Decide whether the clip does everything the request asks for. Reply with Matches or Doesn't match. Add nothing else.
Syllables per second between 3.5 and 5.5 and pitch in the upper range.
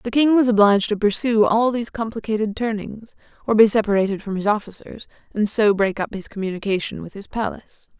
Doesn't match